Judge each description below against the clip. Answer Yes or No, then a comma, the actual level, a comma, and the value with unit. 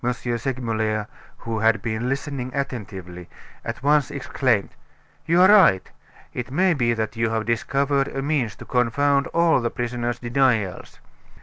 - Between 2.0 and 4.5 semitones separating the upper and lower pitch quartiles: Yes, average, 3.6 semitones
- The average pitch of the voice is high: No, low, 125 Hz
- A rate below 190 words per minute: Yes, average, 140 wpm